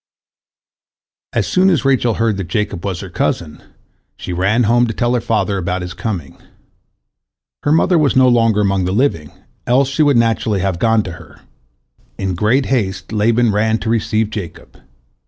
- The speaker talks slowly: No, average, 175 wpm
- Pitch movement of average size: Yes, average, 4.0 semitones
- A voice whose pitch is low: Yes, low, 110 Hz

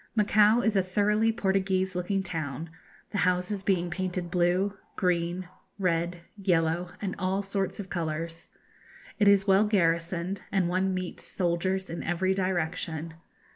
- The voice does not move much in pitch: Yes, narrow, 2.2 semitones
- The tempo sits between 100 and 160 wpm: Yes, slow, 135 wpm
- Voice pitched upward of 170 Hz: Yes, medium, 185 Hz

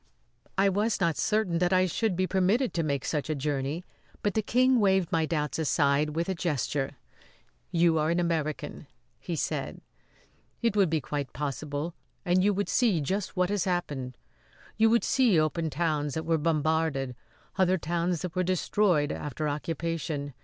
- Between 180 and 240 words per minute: No, average, 170 wpm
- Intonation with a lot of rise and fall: No, average, 3.9 semitones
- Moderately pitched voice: Yes, medium, 165 Hz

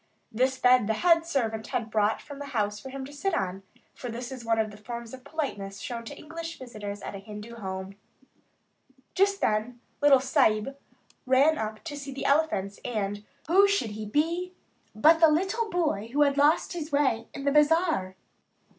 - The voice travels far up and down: Yes, wide, 6.0 semitones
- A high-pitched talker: Yes, very high, 260 Hz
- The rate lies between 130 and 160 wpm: No, average, 190 wpm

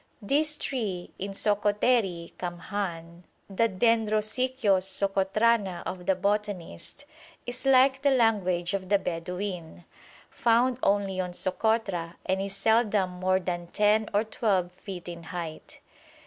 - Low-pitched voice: No, high, 195 Hz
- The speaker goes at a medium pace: No, slow, 120 wpm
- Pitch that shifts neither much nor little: Yes, average, 3.6 semitones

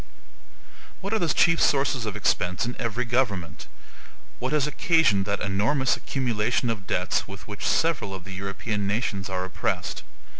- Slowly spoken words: No, average, 155 wpm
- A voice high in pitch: No, low, 110 Hz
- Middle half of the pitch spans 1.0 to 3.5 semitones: No, average, 5.2 semitones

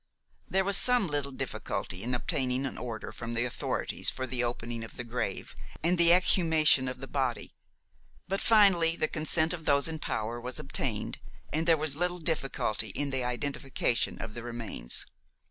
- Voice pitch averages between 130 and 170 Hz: Yes, low, 135 Hz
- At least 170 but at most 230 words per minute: Yes, average, 175 wpm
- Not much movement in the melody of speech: No, average, 5.2 semitones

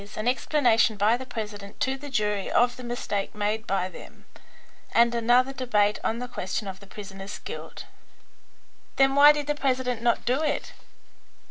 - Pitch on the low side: No, high, 235 Hz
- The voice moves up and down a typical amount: Yes, average, 3.8 semitones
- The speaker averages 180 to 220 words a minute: No, average, 165 wpm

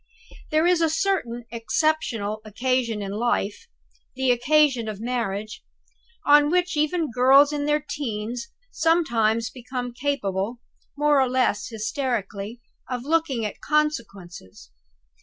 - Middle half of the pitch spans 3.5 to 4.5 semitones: No, average, 5.3 semitones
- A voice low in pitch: No, very high, 250 Hz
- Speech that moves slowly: Yes, slow, 120 wpm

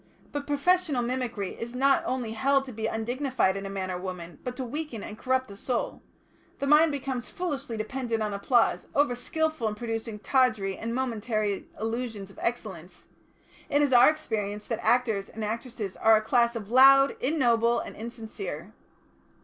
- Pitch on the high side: Yes, high, 235 Hz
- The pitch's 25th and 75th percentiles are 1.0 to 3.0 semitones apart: No, average, 3.7 semitones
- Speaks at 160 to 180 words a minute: Yes, average, 170 wpm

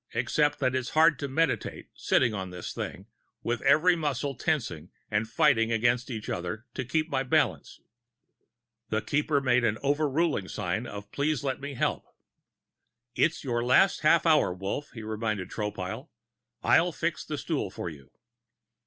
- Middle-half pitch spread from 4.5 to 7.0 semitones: Yes, average, 5.3 semitones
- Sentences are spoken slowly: No, average, 155 wpm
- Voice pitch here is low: Yes, low, 125 Hz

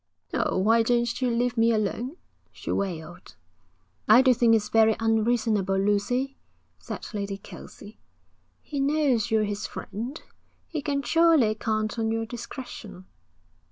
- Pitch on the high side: Yes, high, 225 Hz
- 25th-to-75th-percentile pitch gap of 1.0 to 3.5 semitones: Yes, average, 2.9 semitones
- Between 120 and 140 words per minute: Yes, slow, 135 wpm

